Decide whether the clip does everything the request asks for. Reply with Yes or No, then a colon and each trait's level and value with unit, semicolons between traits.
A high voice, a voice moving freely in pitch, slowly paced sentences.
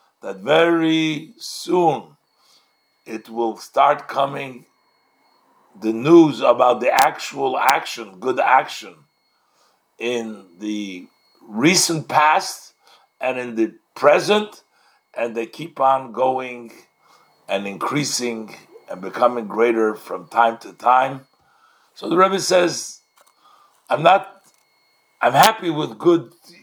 No: low, 130 Hz; wide, 6.5 semitones; slow, 105 wpm